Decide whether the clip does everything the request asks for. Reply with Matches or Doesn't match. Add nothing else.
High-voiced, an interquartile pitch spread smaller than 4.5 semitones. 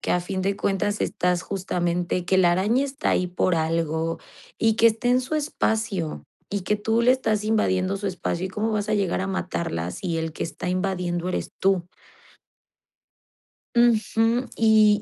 Matches